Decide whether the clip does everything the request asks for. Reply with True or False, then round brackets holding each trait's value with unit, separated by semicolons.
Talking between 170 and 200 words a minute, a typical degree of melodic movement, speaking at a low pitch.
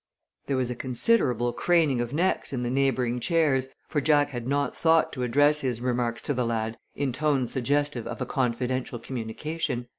True (180 wpm; 3.1 semitones; 130 Hz)